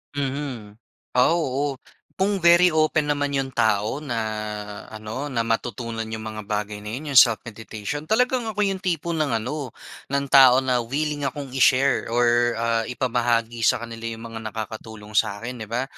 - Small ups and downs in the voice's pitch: No, average, 4.3 semitones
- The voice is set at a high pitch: No, low, 125 Hz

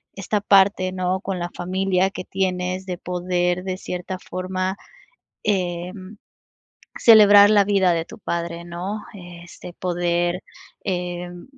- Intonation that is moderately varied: No, narrow, 1.5 semitones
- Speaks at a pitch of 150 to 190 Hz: Yes, medium, 185 Hz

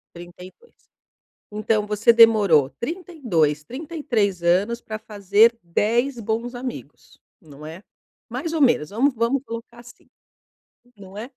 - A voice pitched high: Yes, high, 220 Hz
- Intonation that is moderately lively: Yes, average, 4.5 semitones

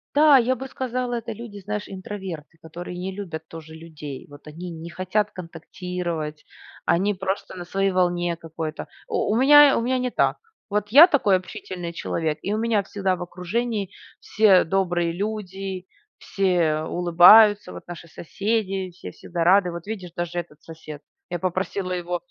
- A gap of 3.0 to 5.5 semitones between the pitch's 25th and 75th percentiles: Yes, average, 3.5 semitones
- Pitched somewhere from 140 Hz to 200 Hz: Yes, medium, 185 Hz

